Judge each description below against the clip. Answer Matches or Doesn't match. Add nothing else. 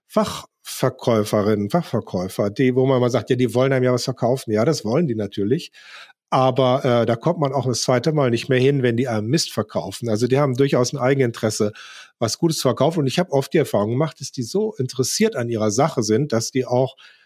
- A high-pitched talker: Doesn't match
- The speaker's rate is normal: Doesn't match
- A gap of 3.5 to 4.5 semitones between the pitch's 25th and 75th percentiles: Doesn't match